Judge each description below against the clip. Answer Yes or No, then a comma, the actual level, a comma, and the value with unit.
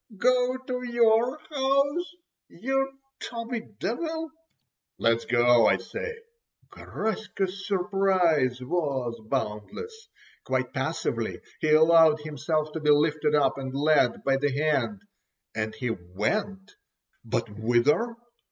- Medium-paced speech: No, slow, 105 wpm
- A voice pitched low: No, medium, 165 Hz